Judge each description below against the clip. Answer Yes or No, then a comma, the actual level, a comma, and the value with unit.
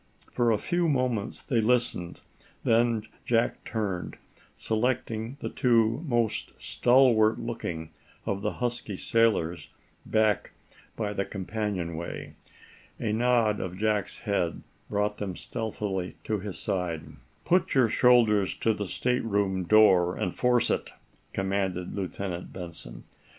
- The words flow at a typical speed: No, slow, 120 wpm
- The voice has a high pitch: No, low, 105 Hz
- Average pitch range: Yes, average, 3.8 semitones